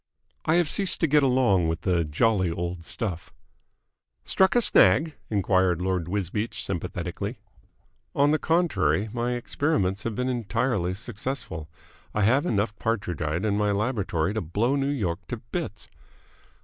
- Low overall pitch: Yes, low, 105 Hz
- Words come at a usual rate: Yes, average, 145 wpm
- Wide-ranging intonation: Yes, wide, 6.1 semitones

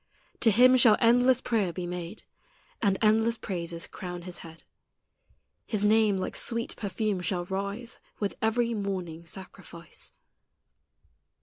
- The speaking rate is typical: No, slow, 125 wpm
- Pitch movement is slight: No, average, 4.1 semitones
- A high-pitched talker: Yes, high, 200 Hz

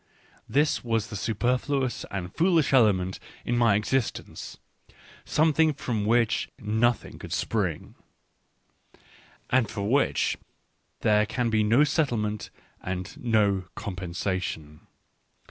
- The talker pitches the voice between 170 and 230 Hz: No, low, 110 Hz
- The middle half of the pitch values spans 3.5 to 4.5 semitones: Yes, average, 4.1 semitones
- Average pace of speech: No, slow, 105 wpm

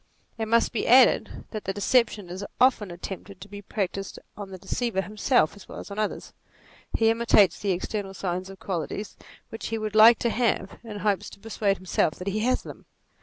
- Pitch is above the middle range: Yes, high, 205 Hz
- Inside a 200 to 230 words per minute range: Yes, fast, 205 wpm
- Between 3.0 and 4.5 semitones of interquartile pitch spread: No, narrow, 2.6 semitones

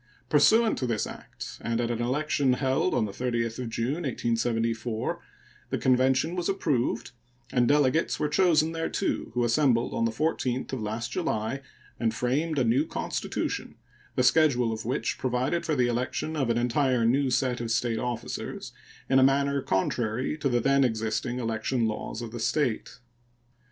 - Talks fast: No, average, 165 wpm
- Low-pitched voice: Yes, low, 125 Hz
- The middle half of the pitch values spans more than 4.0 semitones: No, average, 3.3 semitones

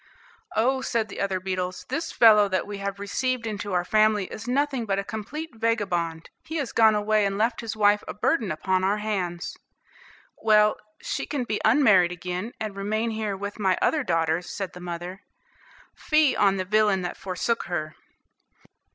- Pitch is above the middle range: Yes, high, 205 Hz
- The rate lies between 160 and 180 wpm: Yes, average, 175 wpm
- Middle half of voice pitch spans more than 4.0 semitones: No, average, 3.3 semitones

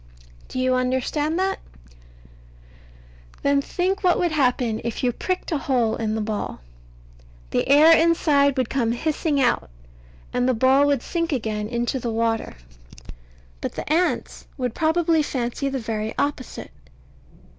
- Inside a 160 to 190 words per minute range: No, average, 145 wpm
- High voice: Yes, very high, 265 Hz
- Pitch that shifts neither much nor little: Yes, average, 4.8 semitones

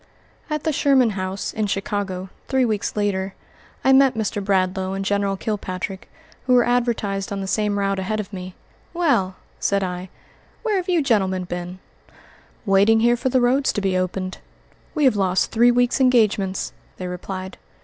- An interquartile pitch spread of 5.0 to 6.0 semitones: No, average, 4.3 semitones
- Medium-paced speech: Yes, average, 170 wpm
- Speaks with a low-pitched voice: No, high, 200 Hz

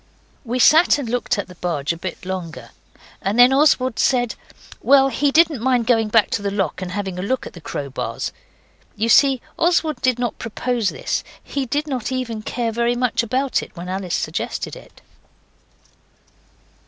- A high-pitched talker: Yes, high, 235 Hz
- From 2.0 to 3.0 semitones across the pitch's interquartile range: No, average, 5.1 semitones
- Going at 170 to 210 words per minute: Yes, average, 180 wpm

